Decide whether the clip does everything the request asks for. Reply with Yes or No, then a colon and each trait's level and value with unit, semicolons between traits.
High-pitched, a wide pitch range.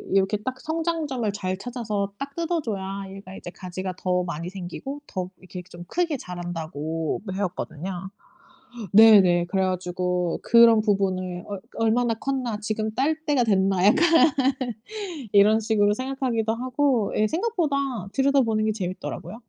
No: high, 210 Hz; average, 5.0 semitones